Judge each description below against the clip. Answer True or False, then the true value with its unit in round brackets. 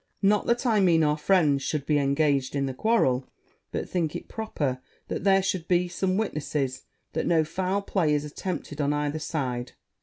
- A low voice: False (155 Hz)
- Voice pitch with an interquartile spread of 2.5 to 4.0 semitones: False (4.8 semitones)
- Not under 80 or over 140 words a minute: False (185 wpm)